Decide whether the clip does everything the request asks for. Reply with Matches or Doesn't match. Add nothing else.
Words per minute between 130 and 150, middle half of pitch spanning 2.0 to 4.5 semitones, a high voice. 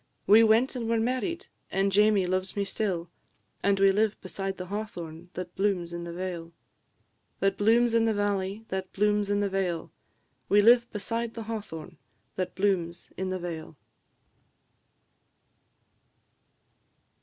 Matches